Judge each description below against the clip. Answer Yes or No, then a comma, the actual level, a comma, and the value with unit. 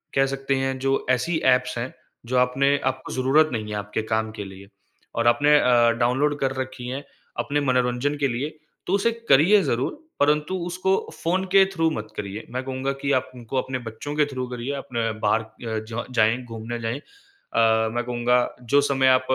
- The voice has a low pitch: Yes, low, 130 Hz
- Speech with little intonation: No, average, 3.3 semitones